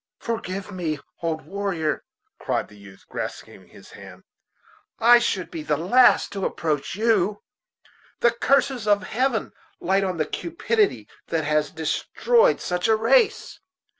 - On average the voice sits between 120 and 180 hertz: No, high, 195 Hz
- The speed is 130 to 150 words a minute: Yes, slow, 135 wpm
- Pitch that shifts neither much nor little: No, wide, 6.6 semitones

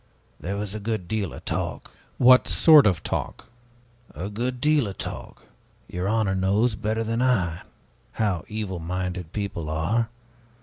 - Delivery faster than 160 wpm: No, average, 150 wpm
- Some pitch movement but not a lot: Yes, average, 3.7 semitones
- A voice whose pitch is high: No, low, 105 Hz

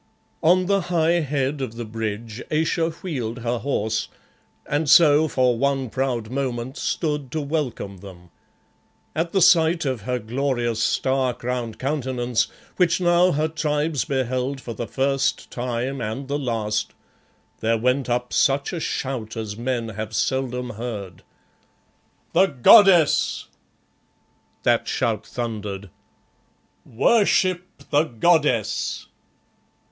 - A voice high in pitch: No, low, 130 Hz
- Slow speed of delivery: Yes, slow, 120 wpm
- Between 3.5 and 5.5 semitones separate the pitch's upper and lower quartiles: Yes, average, 4.8 semitones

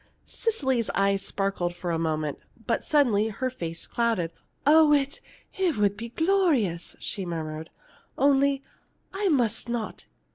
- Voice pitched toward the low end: No, high, 230 Hz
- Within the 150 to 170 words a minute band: No, slow, 135 wpm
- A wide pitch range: Yes, wide, 8.2 semitones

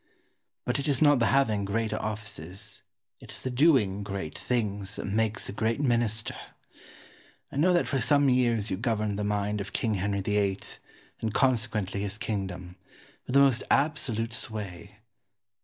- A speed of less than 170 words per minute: Yes, average, 160 wpm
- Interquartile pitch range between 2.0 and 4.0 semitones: Yes, average, 3.5 semitones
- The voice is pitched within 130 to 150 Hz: No, low, 110 Hz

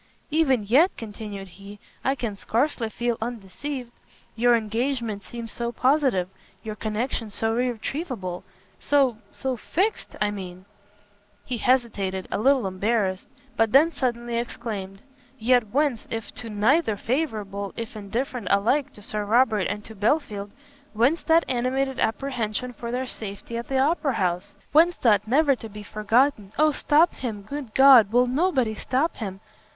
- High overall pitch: Yes, high, 235 Hz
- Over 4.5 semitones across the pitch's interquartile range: No, average, 4.1 semitones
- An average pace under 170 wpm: Yes, average, 150 wpm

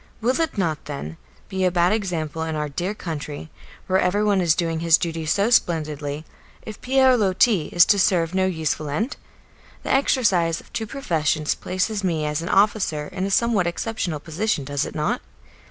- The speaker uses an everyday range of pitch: Yes, average, 4.7 semitones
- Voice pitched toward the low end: No, medium, 175 Hz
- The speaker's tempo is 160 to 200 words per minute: Yes, average, 180 wpm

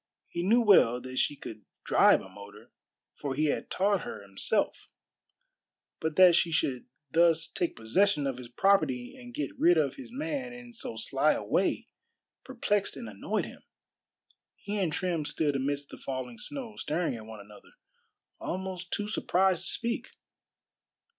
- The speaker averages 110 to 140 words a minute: No, average, 160 wpm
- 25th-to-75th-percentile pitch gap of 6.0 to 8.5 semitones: Yes, wide, 7.8 semitones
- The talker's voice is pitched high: No, medium, 165 Hz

